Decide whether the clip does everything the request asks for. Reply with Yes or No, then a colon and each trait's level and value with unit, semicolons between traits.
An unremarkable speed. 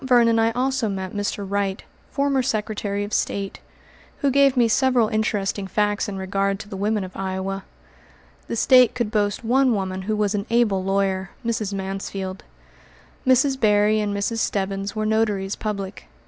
Yes: average, 160 wpm